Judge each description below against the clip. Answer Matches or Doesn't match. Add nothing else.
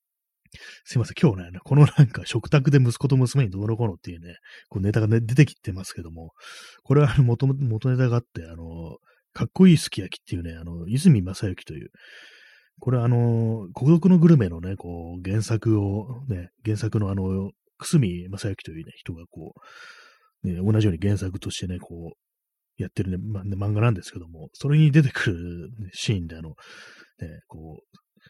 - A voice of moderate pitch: Doesn't match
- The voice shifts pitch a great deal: Matches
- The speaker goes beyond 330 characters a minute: Matches